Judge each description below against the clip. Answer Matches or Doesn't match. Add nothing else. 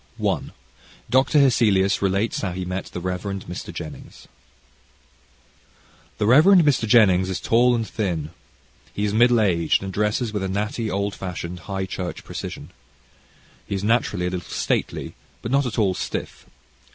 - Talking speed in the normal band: Matches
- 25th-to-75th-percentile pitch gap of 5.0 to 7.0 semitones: Doesn't match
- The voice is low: Matches